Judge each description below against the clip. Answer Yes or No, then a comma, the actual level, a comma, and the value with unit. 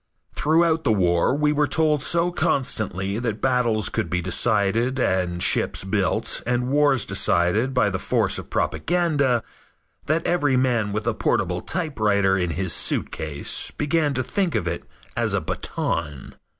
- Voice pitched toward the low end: Yes, low, 120 Hz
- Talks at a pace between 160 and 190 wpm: No, average, 150 wpm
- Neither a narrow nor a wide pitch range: No, wide, 7.4 semitones